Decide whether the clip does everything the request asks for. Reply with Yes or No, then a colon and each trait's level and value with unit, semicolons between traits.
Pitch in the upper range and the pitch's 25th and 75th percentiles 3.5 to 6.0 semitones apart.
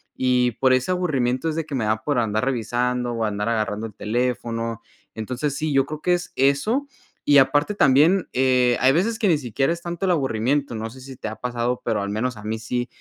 No: low, 125 Hz; average, 4.2 semitones